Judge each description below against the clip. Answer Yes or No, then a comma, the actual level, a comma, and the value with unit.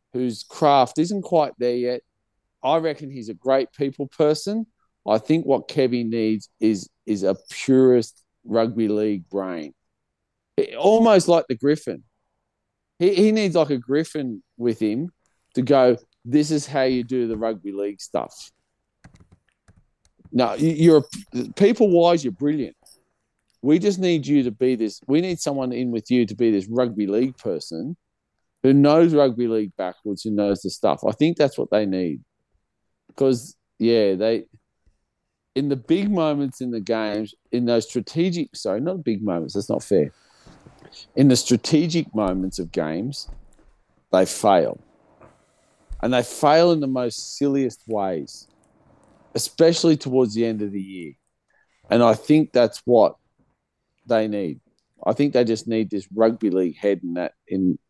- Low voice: Yes, low, 125 Hz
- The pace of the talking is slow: No, average, 155 wpm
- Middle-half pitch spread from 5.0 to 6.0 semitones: Yes, wide, 5.4 semitones